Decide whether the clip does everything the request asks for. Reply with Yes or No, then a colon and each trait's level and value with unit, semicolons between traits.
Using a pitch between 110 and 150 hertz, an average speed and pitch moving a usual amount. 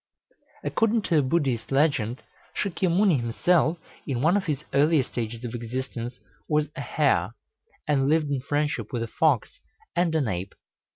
Yes: medium, 140 Hz; average, 155 wpm; average, 5.0 semitones